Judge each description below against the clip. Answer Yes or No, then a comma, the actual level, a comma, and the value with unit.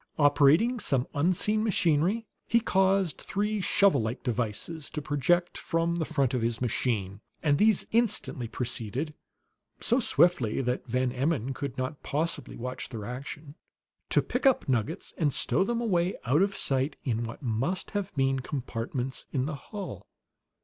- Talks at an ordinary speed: Yes, average, 155 wpm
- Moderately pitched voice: Yes, medium, 145 Hz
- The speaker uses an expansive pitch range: Yes, wide, 6.6 semitones